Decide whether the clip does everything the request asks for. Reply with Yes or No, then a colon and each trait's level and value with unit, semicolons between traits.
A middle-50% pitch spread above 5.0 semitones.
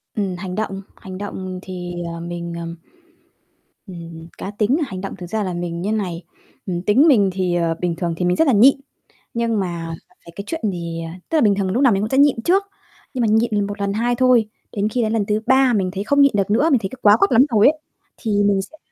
No: average, 4.5 semitones